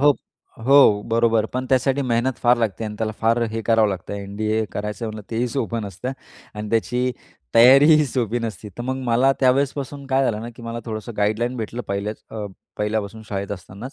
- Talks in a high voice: No, low, 115 Hz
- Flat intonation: No, average, 3.0 semitones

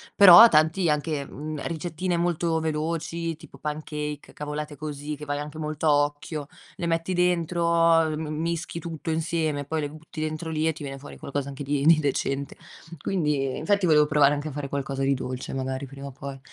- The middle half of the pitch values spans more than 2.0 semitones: Yes, narrow, 2.4 semitones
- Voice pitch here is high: No, medium, 155 Hz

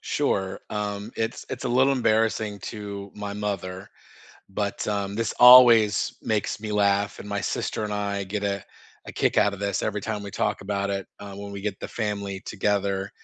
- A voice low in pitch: Yes, low, 100 Hz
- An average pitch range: No, narrow, 1.1 semitones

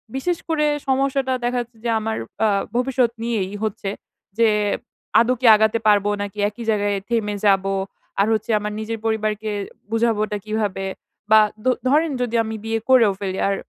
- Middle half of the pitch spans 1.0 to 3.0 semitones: Yes, average, 2.7 semitones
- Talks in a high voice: Yes, high, 220 Hz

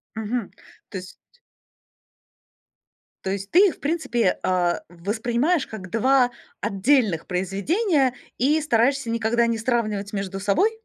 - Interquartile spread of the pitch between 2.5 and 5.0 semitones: No, wide, 5.5 semitones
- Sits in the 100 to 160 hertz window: No, high, 230 Hz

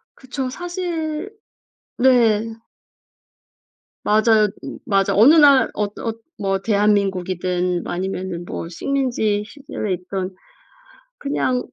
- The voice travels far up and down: Yes, wide, 5.7 semitones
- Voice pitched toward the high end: Yes, high, 215 Hz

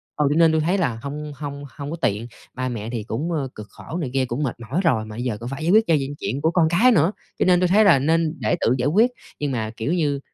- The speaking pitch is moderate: Yes, medium, 145 Hz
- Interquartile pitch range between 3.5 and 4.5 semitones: No, average, 5.2 semitones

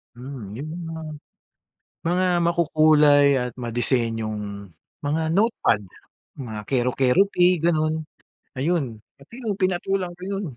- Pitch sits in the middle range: Yes, medium, 145 Hz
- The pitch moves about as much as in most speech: No, wide, 6.4 semitones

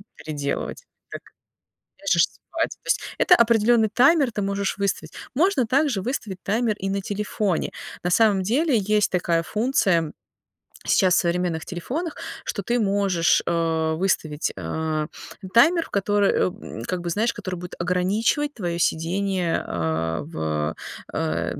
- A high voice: Yes, high, 195 Hz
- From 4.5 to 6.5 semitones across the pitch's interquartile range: Yes, average, 4.8 semitones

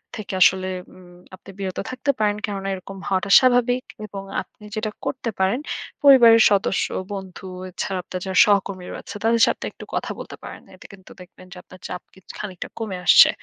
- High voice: Yes, high, 195 Hz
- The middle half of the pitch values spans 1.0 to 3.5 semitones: Yes, average, 3.1 semitones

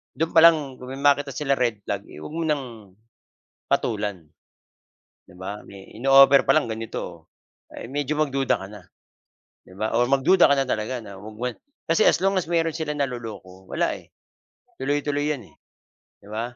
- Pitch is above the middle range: No, low, 135 Hz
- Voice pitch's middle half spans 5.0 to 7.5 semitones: Yes, average, 5.3 semitones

